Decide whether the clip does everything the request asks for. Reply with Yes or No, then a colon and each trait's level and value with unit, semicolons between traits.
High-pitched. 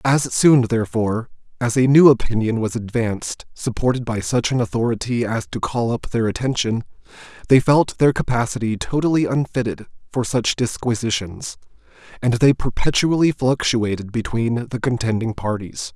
No: low, 120 Hz